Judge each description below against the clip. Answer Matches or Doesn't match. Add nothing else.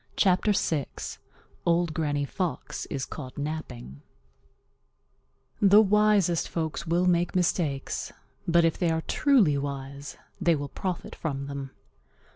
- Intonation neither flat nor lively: Matches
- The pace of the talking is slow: Matches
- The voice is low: Doesn't match